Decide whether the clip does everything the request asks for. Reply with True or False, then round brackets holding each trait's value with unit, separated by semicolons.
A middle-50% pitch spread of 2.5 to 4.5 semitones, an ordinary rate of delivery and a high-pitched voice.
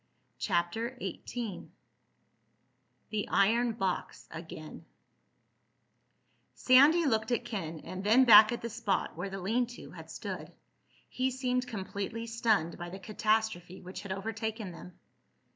False (4.0 semitones; 125 wpm; 215 Hz)